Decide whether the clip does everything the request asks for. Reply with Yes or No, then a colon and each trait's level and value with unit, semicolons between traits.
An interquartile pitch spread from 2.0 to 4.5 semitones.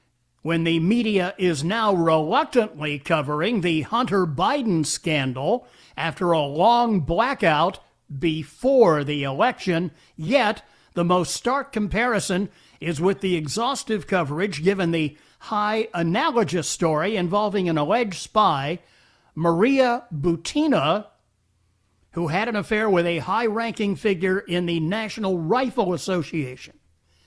No: average, 5.2 semitones